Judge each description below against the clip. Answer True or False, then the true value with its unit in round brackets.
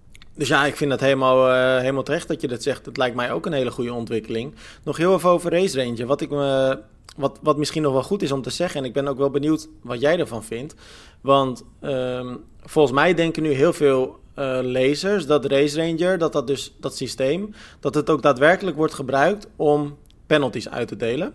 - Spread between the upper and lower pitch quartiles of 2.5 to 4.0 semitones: True (3.1 semitones)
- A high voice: False (140 Hz)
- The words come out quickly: True (220 wpm)